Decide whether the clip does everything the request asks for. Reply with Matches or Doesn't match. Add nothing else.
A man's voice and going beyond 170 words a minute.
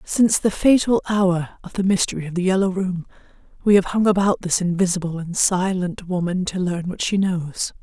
Doesn't match